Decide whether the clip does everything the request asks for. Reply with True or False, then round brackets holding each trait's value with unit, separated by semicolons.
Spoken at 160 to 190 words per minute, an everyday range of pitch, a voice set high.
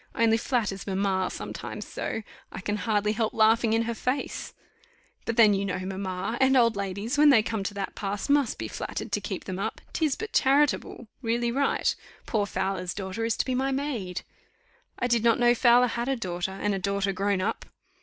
False (200 wpm; 3.6 semitones; 220 Hz)